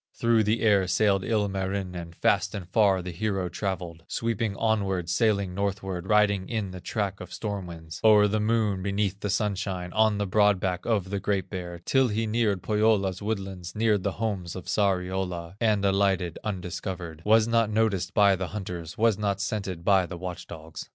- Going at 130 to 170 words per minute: No, average, 180 wpm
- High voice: No, low, 100 Hz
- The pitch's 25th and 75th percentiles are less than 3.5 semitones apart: Yes, narrow, 2.6 semitones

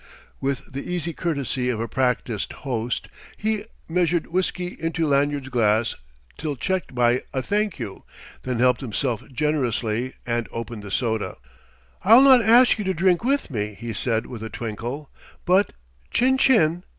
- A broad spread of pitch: Yes, wide, 7.1 semitones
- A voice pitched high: No, low, 135 Hz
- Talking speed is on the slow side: No, average, 155 wpm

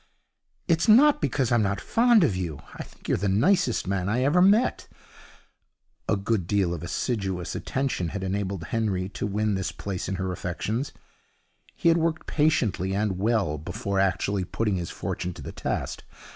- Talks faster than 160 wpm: Yes, average, 170 wpm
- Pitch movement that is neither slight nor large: No, wide, 6.0 semitones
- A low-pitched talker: Yes, low, 100 Hz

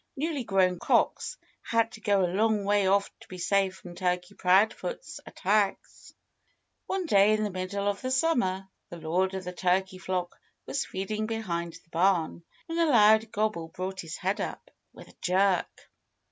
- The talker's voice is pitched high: Yes, high, 195 Hz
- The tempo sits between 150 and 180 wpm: Yes, average, 175 wpm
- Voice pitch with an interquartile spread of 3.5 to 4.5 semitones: No, average, 2.8 semitones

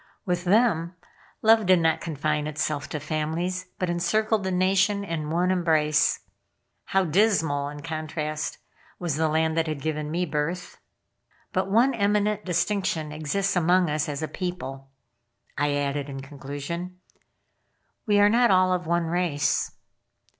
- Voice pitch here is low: No, medium, 170 Hz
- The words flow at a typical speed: Yes, average, 145 wpm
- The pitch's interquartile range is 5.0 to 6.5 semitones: No, average, 3.5 semitones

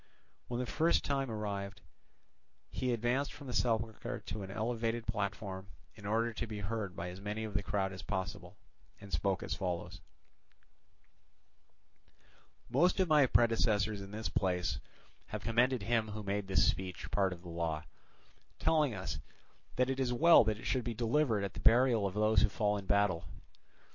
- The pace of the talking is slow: No, average, 175 wpm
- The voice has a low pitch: Yes, low, 105 Hz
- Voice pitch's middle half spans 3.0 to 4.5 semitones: Yes, average, 3.4 semitones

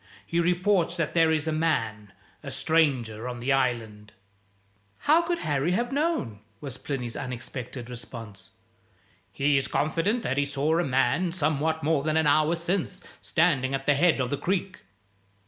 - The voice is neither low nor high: Yes, medium, 150 Hz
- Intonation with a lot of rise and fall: No, average, 5.0 semitones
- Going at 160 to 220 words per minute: Yes, average, 165 wpm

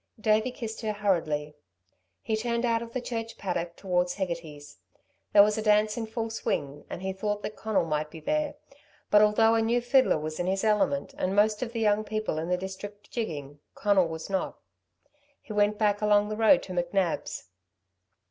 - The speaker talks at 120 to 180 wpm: No, average, 190 wpm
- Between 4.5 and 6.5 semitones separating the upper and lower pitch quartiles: No, average, 3.8 semitones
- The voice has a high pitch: Yes, high, 210 Hz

